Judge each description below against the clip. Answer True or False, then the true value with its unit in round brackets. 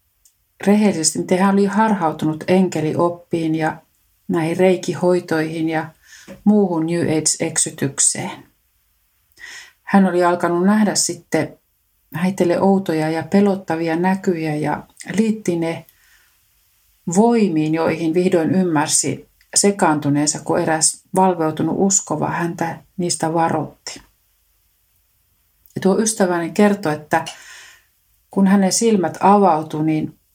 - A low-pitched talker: False (165 Hz)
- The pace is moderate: False (90 wpm)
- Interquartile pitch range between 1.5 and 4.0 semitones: True (3.4 semitones)